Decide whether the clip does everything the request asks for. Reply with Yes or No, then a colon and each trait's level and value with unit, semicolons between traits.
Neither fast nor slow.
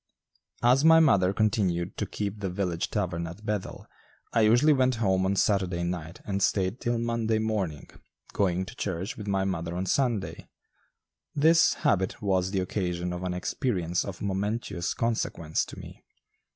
Yes: average, 160 wpm